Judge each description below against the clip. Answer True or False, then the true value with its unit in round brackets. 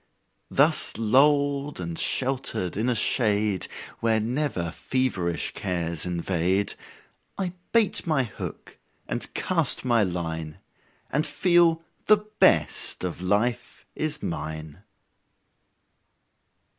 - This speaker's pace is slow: True (100 wpm)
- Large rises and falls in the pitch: True (8.3 semitones)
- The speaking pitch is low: True (110 Hz)